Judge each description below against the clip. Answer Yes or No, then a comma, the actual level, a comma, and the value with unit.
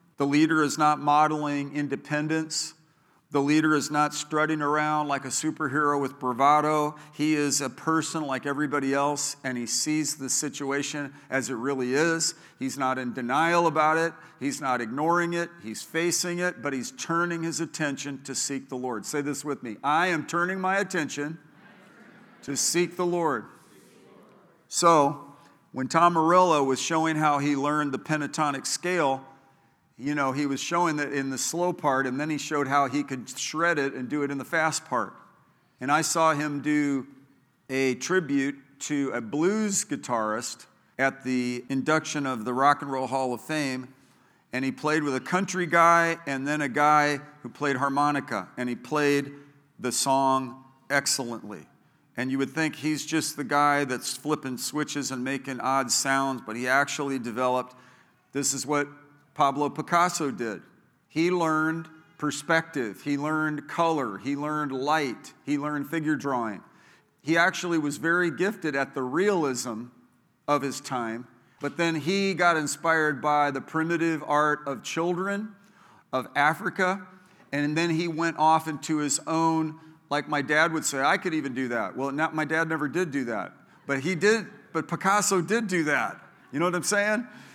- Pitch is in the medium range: Yes, medium, 145 Hz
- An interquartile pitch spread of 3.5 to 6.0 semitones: No, average, 2.9 semitones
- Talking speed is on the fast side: No, average, 170 wpm